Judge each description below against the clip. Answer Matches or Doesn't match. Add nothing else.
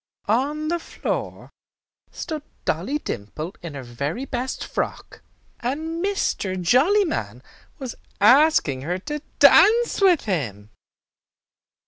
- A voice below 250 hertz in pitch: Doesn't match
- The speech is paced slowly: Matches